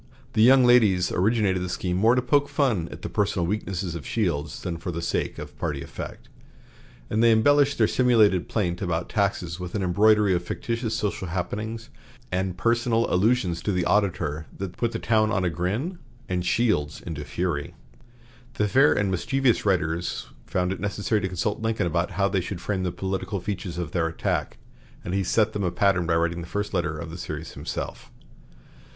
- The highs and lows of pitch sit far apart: No, average, 4.1 semitones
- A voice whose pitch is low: Yes, very low, 95 Hz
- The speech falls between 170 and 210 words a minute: Yes, average, 190 wpm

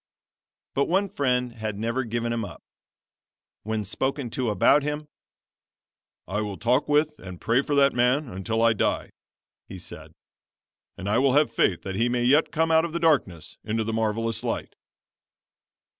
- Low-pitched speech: Yes, low, 120 Hz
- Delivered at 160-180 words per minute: Yes, average, 165 wpm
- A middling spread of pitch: Yes, average, 4.5 semitones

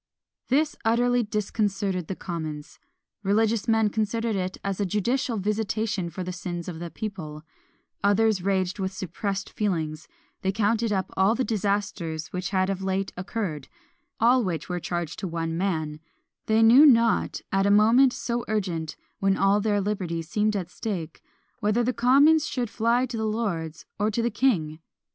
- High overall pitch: Yes, high, 200 Hz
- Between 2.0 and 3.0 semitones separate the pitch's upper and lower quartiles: No, average, 3.8 semitones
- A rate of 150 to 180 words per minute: Yes, average, 165 wpm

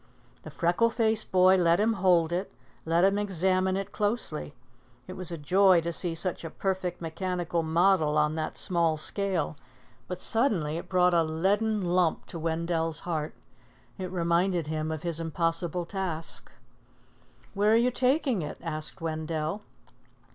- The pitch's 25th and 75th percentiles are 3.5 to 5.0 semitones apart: No, average, 2.8 semitones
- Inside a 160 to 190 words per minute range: No, average, 150 wpm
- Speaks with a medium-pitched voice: Yes, medium, 175 Hz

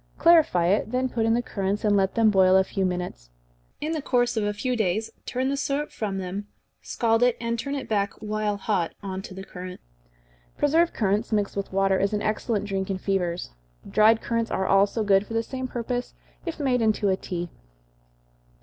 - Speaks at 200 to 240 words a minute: Yes, fast, 205 wpm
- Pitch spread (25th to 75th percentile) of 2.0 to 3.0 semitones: No, average, 3.7 semitones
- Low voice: No, high, 210 Hz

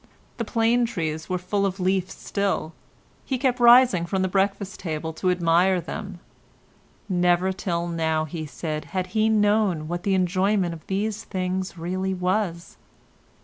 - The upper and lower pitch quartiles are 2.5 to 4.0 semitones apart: Yes, average, 2.8 semitones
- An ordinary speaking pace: Yes, average, 150 wpm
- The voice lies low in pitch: No, medium, 185 Hz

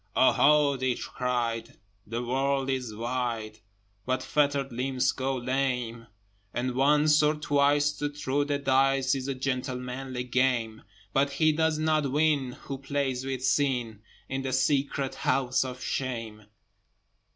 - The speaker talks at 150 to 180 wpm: No, slow, 135 wpm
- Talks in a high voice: No, low, 130 Hz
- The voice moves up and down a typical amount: No, narrow, 2.1 semitones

